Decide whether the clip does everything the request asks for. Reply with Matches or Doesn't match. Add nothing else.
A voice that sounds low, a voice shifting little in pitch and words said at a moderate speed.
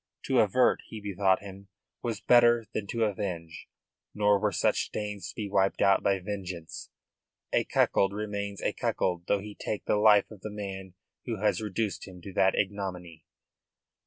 Matches